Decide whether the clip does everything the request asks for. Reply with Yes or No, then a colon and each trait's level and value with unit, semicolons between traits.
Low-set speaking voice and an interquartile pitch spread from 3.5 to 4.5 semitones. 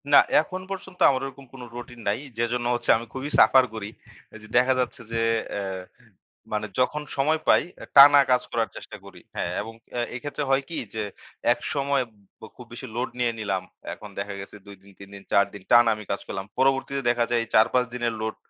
Yes: low, 120 Hz; average, 3.9 semitones